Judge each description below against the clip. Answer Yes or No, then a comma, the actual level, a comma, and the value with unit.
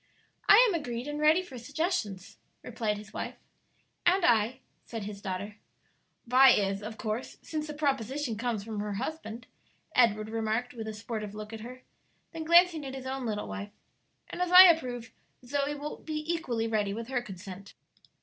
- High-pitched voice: Yes, high, 240 Hz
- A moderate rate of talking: Yes, average, 175 wpm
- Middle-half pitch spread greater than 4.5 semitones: Yes, wide, 5.6 semitones